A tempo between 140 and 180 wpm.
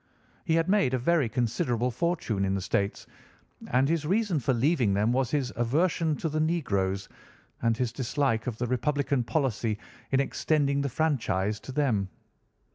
Yes: average, 165 wpm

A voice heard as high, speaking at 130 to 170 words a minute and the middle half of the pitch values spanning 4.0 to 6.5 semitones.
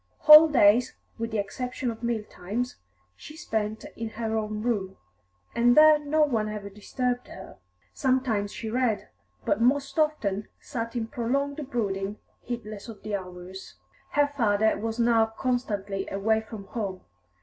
No: high, 225 Hz; average, 150 wpm; average, 3.3 semitones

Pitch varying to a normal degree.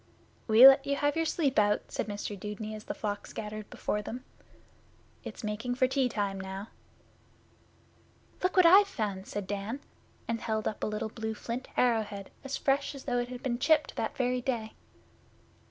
Yes: average, 4.2 semitones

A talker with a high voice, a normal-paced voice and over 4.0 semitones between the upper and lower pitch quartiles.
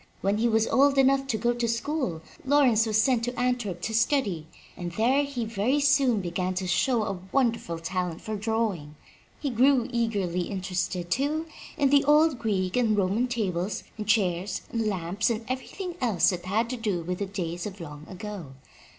Yes: high, 220 Hz; average, 180 wpm; average, 5.2 semitones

